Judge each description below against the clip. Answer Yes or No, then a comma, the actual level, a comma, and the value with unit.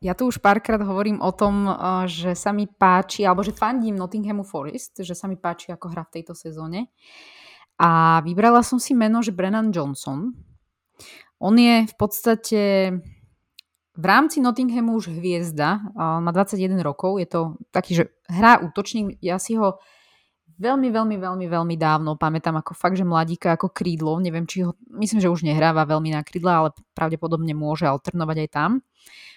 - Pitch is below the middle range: No, medium, 185 Hz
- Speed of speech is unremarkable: No, fast, 170 wpm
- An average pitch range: Yes, average, 4.5 semitones